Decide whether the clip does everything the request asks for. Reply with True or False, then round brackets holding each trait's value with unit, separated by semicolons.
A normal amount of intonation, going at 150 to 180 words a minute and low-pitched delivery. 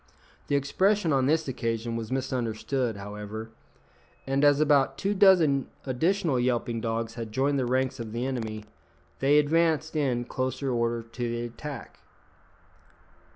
False (3.7 semitones; 140 wpm; 130 Hz)